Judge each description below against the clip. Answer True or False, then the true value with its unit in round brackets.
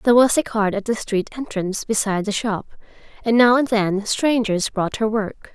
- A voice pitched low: False (220 Hz)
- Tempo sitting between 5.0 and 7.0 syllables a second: True (5.2 syllables/s)